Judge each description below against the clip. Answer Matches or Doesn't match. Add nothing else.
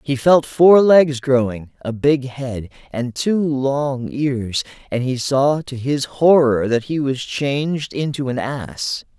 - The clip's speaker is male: Matches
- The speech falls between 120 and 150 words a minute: Doesn't match